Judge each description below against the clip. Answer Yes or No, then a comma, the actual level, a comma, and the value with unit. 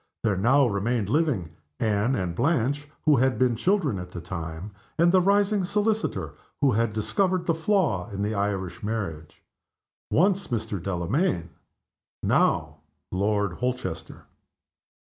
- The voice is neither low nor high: No, low, 115 Hz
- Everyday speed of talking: No, slow, 130 wpm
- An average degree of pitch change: No, wide, 8.7 semitones